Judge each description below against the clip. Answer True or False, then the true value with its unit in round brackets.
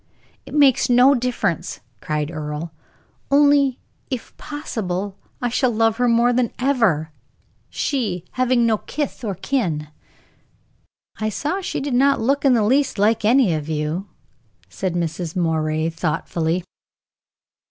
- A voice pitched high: True (225 Hz)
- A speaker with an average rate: False (130 wpm)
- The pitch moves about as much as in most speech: False (7.5 semitones)